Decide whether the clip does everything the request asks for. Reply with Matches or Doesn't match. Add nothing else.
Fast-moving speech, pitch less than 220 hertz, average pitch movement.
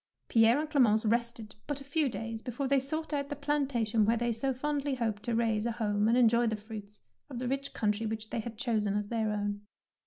Doesn't match